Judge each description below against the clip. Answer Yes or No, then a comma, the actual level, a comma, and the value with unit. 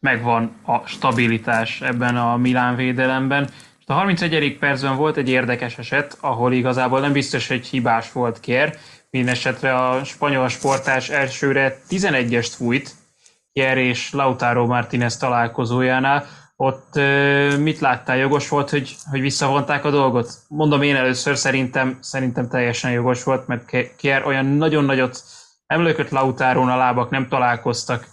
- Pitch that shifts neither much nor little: No, narrow, 2.1 semitones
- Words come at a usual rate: Yes, average, 135 wpm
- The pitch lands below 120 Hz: No, low, 130 Hz